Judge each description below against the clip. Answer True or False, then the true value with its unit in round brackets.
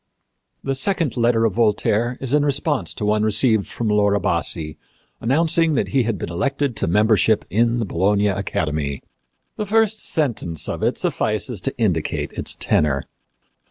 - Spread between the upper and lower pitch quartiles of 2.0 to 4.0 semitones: False (5.2 semitones)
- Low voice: True (115 Hz)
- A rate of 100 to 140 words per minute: False (160 wpm)